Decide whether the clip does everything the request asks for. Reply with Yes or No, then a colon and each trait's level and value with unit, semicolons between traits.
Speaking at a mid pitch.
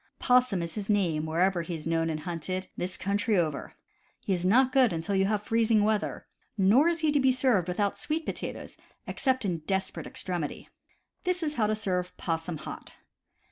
No: high, 195 Hz